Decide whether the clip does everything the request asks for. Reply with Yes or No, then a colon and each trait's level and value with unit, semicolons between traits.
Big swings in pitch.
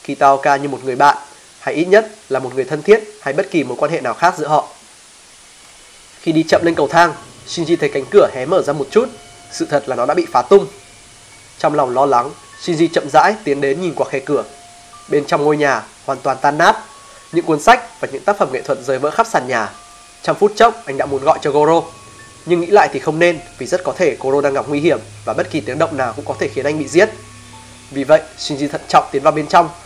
No: average, 4.7 semitones